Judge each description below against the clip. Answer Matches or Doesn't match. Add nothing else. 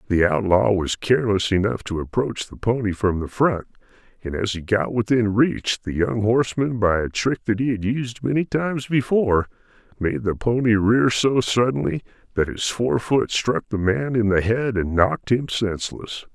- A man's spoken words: Matches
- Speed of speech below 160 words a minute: Doesn't match